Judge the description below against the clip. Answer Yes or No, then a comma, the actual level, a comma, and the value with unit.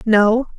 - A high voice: Yes, high, 225 Hz